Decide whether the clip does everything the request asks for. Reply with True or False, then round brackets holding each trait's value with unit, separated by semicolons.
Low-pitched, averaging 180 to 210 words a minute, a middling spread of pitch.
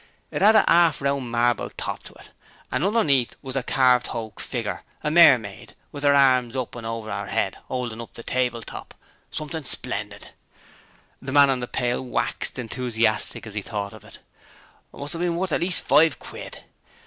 True (130 Hz; 185 wpm; 3.7 semitones)